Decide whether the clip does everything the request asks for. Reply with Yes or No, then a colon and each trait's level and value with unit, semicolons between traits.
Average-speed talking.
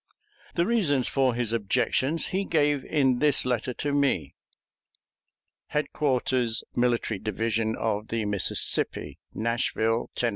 No: slow, 115 wpm